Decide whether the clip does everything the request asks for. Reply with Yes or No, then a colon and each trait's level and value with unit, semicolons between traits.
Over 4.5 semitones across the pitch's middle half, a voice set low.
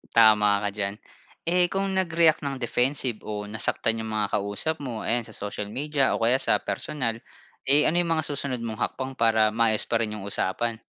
Yes: average, 5.1 semitones; low, 115 Hz